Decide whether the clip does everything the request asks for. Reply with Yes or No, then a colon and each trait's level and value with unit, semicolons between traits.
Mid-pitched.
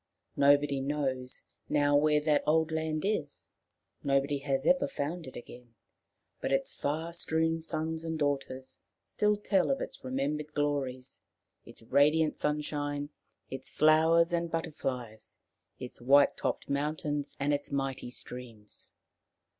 Yes: medium, 145 Hz